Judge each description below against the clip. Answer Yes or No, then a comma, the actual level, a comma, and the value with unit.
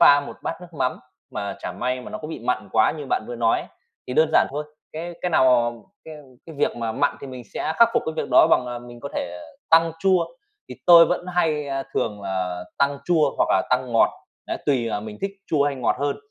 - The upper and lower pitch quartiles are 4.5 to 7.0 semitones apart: Yes, average, 5.2 semitones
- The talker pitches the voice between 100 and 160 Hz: Yes, medium, 140 Hz